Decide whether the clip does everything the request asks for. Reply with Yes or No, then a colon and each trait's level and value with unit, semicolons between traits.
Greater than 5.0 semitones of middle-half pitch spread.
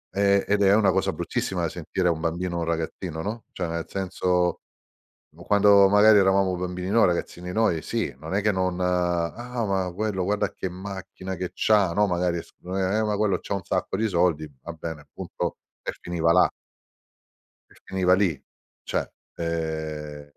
No: average, 2.7 semitones